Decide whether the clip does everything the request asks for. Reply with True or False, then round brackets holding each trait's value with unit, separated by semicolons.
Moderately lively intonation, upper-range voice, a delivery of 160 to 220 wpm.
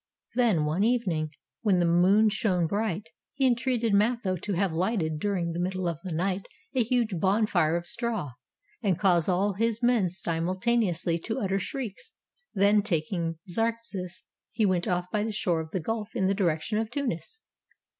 True (4.3 semitones; 195 Hz; 175 wpm)